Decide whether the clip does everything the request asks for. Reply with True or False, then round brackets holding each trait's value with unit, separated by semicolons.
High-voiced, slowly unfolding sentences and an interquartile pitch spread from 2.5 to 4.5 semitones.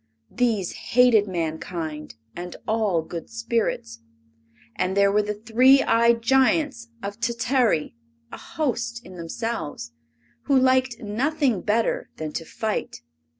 False (225 Hz; 120 wpm; 5.1 semitones)